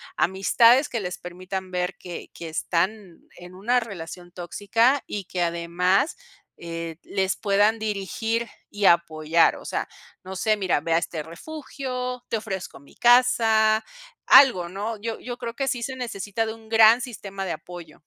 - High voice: Yes, high, 200 Hz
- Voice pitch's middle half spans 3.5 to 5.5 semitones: Yes, average, 4.6 semitones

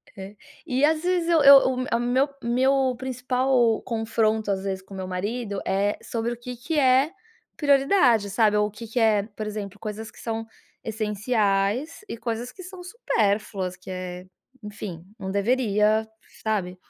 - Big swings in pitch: No, average, 4.1 semitones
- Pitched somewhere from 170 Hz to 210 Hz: No, high, 225 Hz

